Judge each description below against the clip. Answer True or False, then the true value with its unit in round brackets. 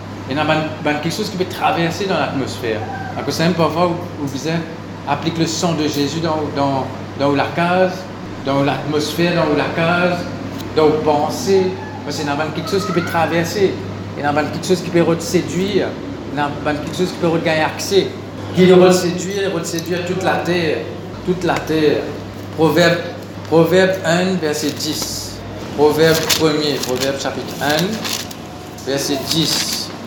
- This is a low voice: False (150 Hz)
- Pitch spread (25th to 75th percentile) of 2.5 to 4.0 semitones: False (4.7 semitones)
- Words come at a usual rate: True (150 wpm)